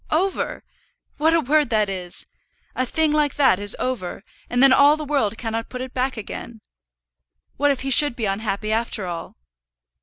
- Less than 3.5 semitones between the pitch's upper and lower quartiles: No, average, 5.1 semitones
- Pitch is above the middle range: Yes, very high, 255 Hz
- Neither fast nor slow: Yes, average, 180 wpm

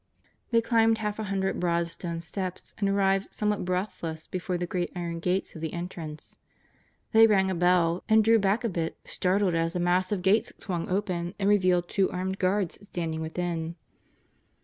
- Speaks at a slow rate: No, average, 175 wpm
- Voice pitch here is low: No, medium, 185 Hz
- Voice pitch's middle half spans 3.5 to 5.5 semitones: No, average, 2.7 semitones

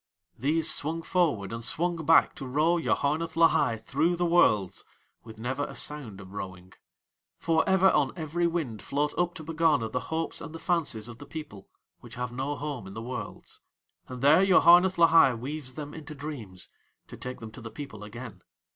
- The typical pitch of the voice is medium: Yes, medium, 145 Hz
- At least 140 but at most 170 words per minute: No, average, 185 wpm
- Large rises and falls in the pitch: Yes, wide, 6.1 semitones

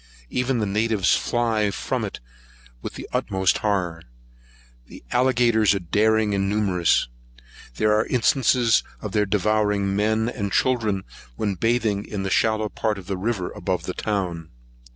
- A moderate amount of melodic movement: No, narrow, 2.3 semitones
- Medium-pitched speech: No, low, 105 Hz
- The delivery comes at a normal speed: Yes, average, 150 wpm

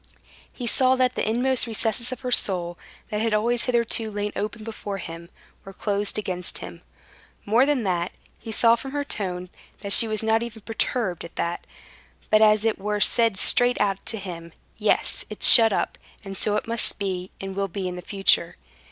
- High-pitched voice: Yes, high, 210 Hz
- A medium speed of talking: Yes, average, 190 wpm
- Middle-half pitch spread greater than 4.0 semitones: No, average, 3.2 semitones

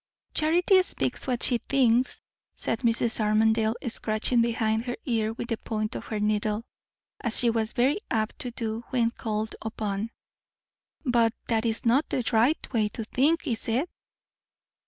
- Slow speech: No, average, 155 wpm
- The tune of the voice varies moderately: No, narrow, 2.0 semitones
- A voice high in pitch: Yes, high, 230 Hz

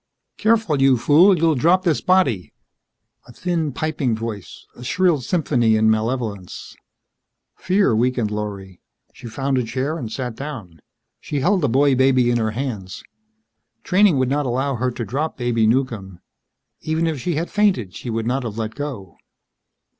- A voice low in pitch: Yes, low, 130 Hz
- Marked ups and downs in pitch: Yes, wide, 5.7 semitones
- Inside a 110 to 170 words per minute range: Yes, average, 160 wpm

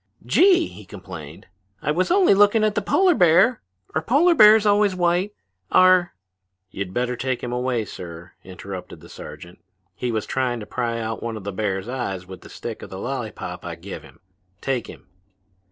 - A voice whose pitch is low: Yes, low, 125 Hz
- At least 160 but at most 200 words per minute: Yes, average, 185 wpm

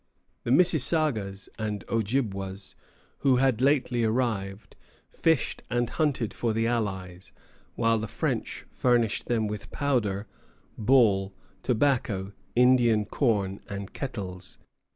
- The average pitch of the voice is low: Yes, low, 115 Hz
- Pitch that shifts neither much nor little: Yes, average, 4.2 semitones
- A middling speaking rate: No, slow, 110 wpm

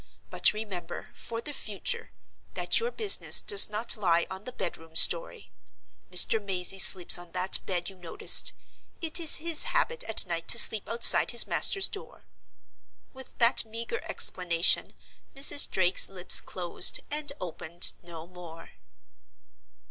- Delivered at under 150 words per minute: Yes, average, 140 wpm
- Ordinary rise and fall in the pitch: No, wide, 7.0 semitones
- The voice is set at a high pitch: Yes, high, 200 Hz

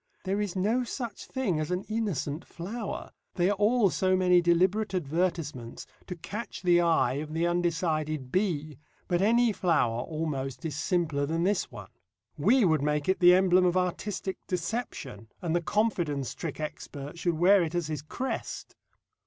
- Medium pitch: Yes, medium, 175 Hz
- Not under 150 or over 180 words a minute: Yes, average, 165 wpm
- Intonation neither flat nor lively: Yes, average, 3.9 semitones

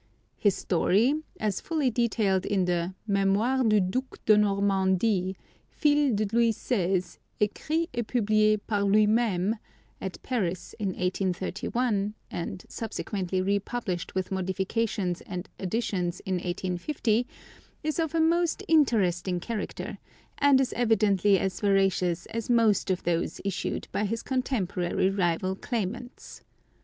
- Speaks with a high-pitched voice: Yes, high, 205 Hz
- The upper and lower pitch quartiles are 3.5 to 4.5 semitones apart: Yes, average, 3.9 semitones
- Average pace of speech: No, slow, 125 wpm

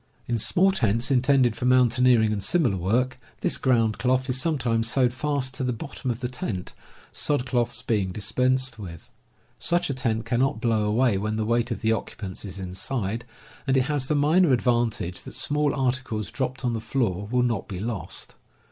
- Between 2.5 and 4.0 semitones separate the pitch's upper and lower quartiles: Yes, average, 2.9 semitones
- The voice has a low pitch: Yes, low, 120 Hz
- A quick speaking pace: No, average, 185 wpm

